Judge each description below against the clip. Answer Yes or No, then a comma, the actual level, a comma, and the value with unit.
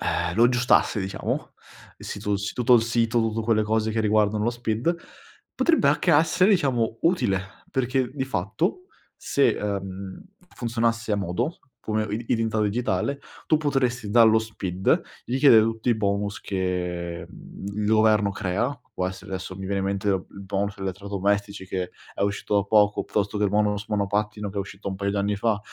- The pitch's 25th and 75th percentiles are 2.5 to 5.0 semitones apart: Yes, average, 2.9 semitones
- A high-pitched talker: No, low, 105 Hz